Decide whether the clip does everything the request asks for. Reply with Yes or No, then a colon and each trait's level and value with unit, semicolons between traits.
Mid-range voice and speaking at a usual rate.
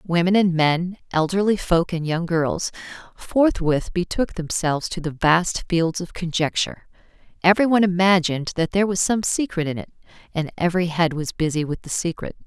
Yes: medium, 175 Hz; average, 165 wpm